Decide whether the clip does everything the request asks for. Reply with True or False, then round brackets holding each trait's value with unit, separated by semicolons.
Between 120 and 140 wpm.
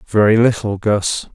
True (135 wpm)